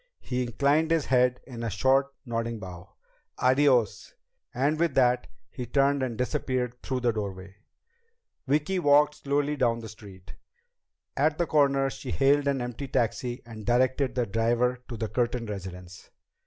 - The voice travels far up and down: No, average, 3.3 semitones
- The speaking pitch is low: Yes, low, 125 Hz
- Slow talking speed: No, average, 155 wpm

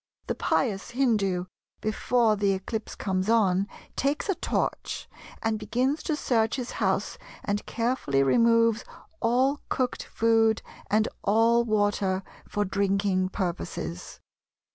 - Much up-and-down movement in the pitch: No, average, 3.2 semitones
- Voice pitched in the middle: No, high, 220 Hz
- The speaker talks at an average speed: No, slow, 120 wpm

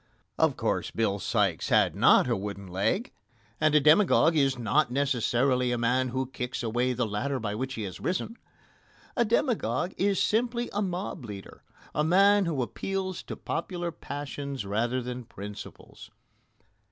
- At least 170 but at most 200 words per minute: No, average, 155 wpm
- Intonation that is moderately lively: No, wide, 7.0 semitones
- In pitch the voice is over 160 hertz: No, low, 130 Hz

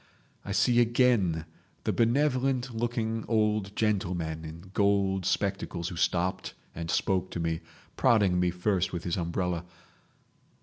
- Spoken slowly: Yes, slow, 125 wpm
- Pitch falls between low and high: No, low, 100 Hz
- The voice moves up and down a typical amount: Yes, average, 4.5 semitones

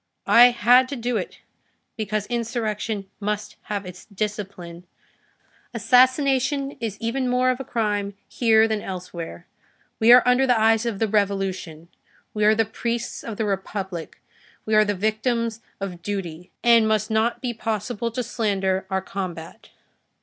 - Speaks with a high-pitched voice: Yes, high, 215 Hz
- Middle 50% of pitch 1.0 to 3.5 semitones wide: Yes, average, 3.2 semitones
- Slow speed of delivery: No, average, 150 wpm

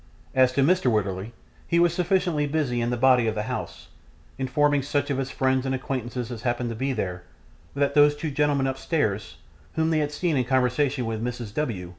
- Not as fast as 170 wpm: No, average, 200 wpm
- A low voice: Yes, low, 130 Hz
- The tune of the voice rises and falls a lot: No, average, 3.6 semitones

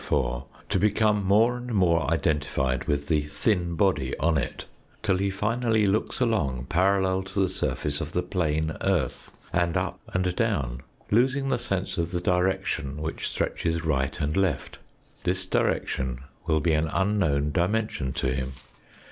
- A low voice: Yes, very low, 85 Hz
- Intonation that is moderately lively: Yes, average, 4.9 semitones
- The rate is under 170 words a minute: Yes, average, 155 wpm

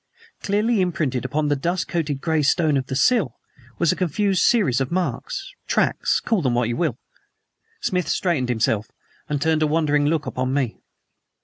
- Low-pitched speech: No, medium, 155 Hz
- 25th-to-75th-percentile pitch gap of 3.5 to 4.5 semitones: No, wide, 5.4 semitones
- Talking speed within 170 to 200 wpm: Yes, average, 175 wpm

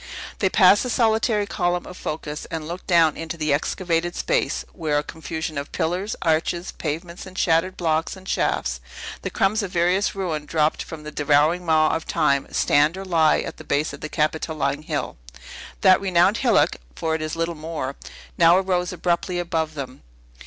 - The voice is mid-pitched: Yes, medium, 165 Hz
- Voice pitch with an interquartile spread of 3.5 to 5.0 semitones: No, average, 3.0 semitones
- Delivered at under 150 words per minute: No, average, 180 wpm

